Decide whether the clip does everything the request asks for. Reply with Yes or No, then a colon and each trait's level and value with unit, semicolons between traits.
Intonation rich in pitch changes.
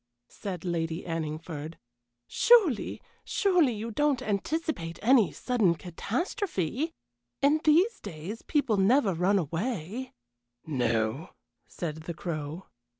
Yes: wide, 8.3 semitones